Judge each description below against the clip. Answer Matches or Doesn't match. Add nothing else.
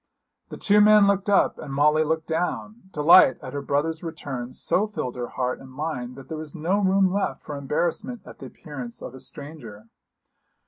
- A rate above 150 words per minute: Matches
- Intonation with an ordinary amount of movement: Doesn't match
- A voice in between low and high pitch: Matches